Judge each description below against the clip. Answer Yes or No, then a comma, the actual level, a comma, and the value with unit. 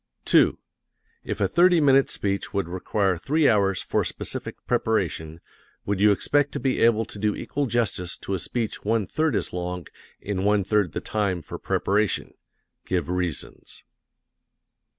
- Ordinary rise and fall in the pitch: Yes, average, 4.2 semitones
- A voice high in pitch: No, low, 100 Hz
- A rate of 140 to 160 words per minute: Yes, average, 155 wpm